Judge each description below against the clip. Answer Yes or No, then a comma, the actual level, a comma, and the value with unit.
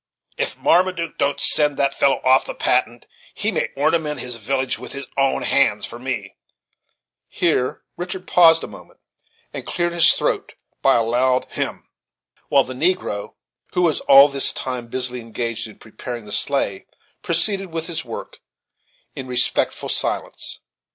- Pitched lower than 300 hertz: Yes, low, 135 Hz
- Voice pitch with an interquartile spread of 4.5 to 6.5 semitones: Yes, average, 4.8 semitones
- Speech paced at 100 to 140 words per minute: No, average, 155 wpm